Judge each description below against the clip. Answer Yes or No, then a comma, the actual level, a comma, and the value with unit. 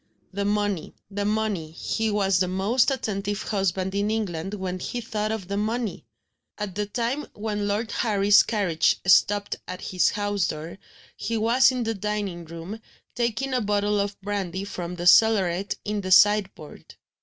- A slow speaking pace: No, average, 165 wpm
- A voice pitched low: No, high, 205 Hz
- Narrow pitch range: Yes, narrow, 2.3 semitones